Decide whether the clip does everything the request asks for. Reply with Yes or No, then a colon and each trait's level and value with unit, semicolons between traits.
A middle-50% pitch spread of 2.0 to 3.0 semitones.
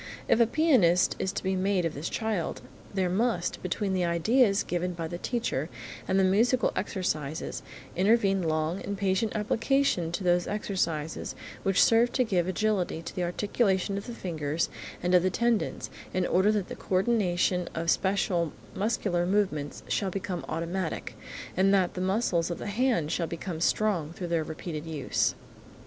No: average, 3.4 semitones